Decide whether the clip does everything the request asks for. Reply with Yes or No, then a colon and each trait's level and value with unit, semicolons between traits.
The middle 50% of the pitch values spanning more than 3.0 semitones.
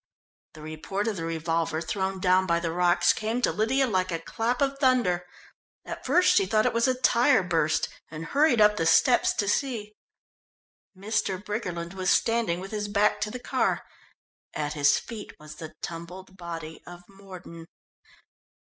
Yes: average, 4.8 semitones